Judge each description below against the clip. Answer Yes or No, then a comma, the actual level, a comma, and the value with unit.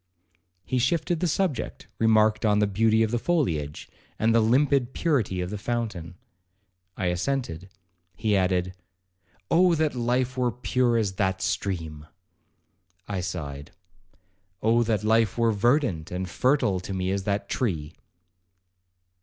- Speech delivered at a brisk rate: No, slow, 135 wpm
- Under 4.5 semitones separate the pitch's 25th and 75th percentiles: No, average, 5.2 semitones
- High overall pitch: No, low, 110 Hz